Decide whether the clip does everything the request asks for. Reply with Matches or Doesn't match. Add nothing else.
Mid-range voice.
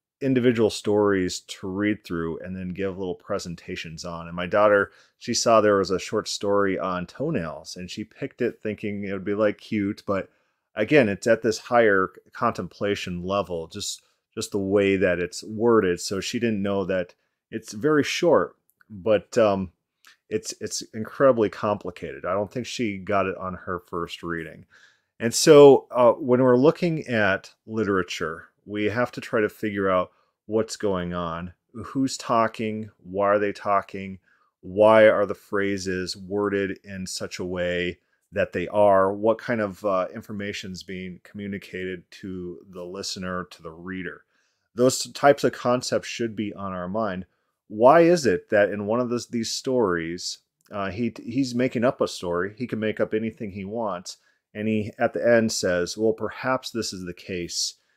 Doesn't match